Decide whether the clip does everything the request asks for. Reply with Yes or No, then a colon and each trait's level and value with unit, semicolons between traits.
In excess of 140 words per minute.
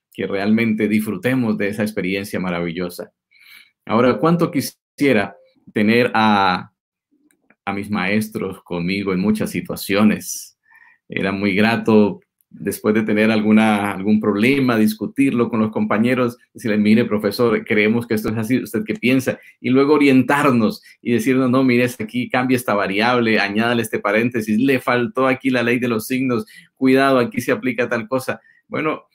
Yes: average, 150 wpm